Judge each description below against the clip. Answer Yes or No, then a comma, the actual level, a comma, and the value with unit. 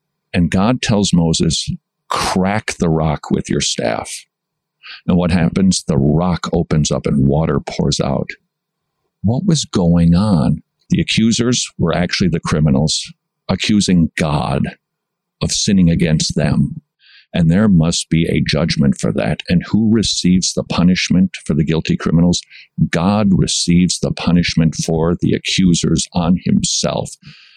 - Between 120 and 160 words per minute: Yes, slow, 135 wpm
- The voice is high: No, very low, 90 Hz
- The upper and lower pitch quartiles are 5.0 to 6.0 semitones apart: Yes, average, 5.3 semitones